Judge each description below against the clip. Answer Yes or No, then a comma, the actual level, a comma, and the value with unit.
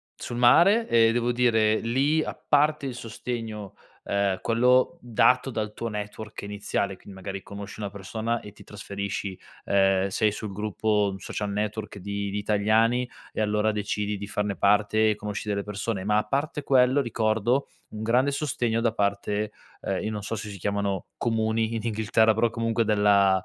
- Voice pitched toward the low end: Yes, low, 110 Hz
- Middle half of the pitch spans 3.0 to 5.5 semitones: No, narrow, 2.4 semitones